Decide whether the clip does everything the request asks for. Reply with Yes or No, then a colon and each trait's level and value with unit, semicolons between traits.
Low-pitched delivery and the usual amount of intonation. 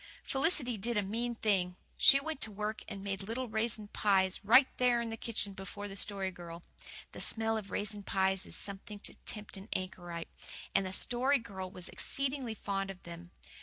No: high, 205 Hz; average, 3.3 semitones